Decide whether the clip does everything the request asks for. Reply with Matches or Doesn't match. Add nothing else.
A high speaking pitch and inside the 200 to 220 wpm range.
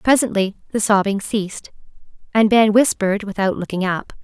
Doesn't match